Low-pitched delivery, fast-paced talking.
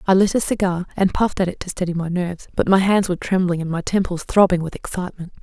No: medium, 185 Hz; fast, 255 wpm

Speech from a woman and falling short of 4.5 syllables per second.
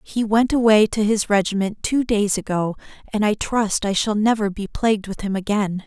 No: female; 5.0 syllables/s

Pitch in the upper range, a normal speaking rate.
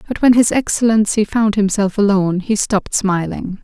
Yes: high, 205 Hz; average, 165 wpm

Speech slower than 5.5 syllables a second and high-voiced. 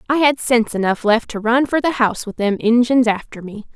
No: 5.7 syllables/s; high, 235 Hz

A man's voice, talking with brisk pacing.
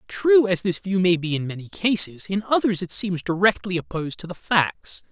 Yes: male; fast, 210 wpm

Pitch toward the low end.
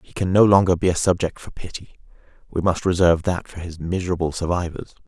Yes: very low, 90 Hz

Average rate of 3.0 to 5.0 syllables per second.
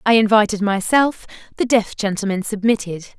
No: 5.3 syllables/s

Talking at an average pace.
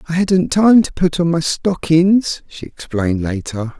Yes: average, 175 wpm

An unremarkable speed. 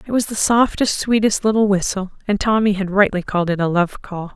No: fast, 220 wpm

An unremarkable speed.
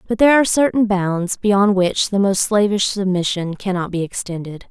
Yes: average, 180 wpm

